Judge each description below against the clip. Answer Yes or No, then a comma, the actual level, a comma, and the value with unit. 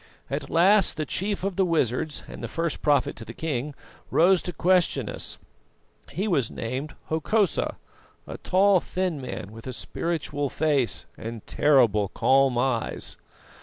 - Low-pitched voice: No, medium, 150 Hz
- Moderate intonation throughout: No, wide, 5.8 semitones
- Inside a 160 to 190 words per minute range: No, average, 150 wpm